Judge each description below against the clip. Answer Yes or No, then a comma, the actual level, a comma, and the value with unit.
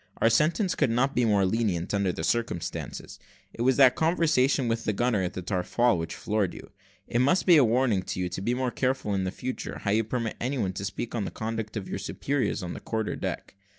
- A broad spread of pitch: No, average, 4.4 semitones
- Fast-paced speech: Yes, fast, 230 wpm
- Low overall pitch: Yes, low, 115 Hz